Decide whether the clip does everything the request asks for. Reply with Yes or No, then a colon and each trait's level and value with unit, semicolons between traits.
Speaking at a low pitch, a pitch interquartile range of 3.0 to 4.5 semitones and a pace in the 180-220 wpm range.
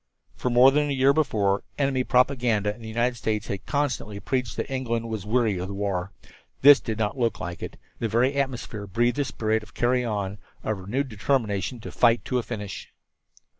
Yes: low, 115 Hz; average, 3.7 semitones; average, 200 wpm